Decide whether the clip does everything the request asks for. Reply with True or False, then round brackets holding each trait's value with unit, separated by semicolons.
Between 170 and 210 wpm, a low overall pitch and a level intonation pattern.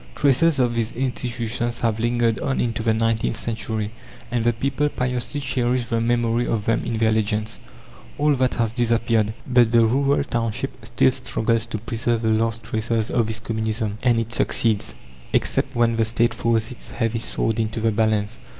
True (175 wpm; 115 Hz; 1.3 semitones)